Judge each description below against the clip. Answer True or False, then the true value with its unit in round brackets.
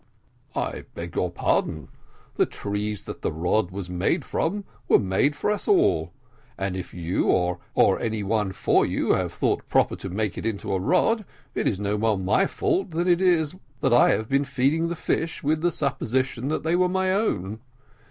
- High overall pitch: False (115 Hz)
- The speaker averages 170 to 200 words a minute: True (190 wpm)